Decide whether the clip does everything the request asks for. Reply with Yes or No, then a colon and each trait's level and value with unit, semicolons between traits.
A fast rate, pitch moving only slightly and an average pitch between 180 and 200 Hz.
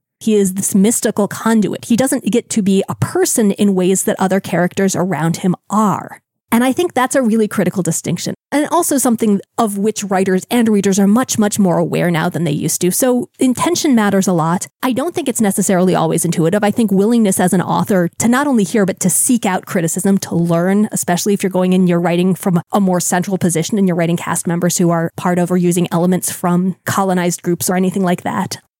No: fast, 220 wpm; average, 3.5 semitones; high, 190 Hz